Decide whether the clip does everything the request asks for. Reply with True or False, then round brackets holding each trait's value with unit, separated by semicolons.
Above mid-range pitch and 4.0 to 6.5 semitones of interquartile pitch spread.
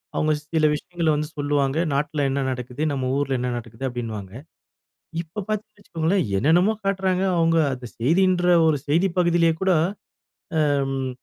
False (155 Hz; 4.7 semitones)